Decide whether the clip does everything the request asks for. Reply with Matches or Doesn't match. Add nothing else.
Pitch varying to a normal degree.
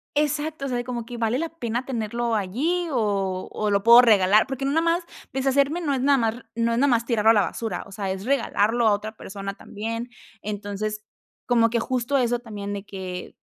Matches